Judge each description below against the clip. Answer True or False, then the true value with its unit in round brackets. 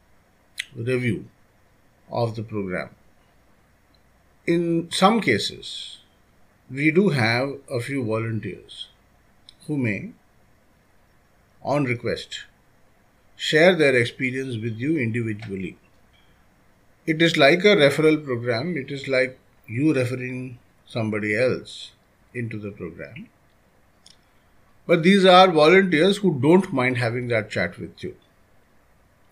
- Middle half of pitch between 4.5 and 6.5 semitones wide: True (5.4 semitones)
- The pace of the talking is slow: True (105 wpm)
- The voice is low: True (115 Hz)